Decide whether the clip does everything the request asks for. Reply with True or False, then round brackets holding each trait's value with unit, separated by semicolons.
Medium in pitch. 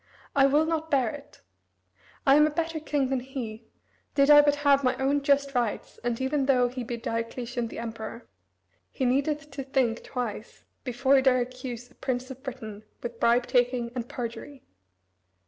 False (260 Hz)